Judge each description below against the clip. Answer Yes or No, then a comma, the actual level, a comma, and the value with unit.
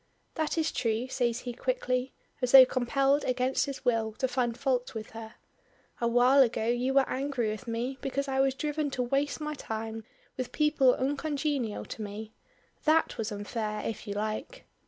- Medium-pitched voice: No, very high, 255 Hz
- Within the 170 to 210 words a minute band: Yes, average, 175 wpm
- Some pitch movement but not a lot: Yes, average, 3.3 semitones